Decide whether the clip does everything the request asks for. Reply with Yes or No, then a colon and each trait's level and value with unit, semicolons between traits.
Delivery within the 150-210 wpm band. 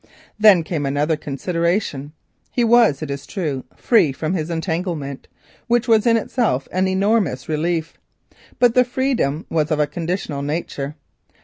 No: slow, 135 wpm